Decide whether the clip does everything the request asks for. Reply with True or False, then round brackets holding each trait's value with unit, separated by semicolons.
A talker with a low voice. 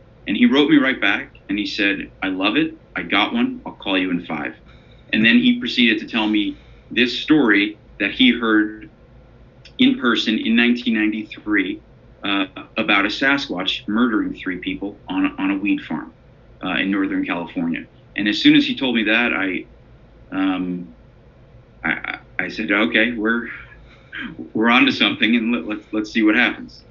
True (125 Hz)